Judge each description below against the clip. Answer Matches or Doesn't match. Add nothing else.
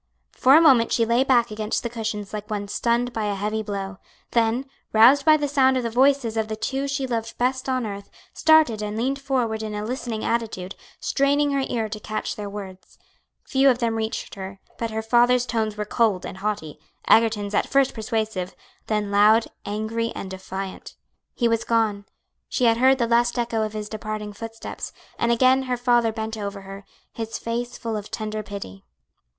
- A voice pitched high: Matches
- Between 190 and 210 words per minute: Matches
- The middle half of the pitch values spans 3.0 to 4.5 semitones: Doesn't match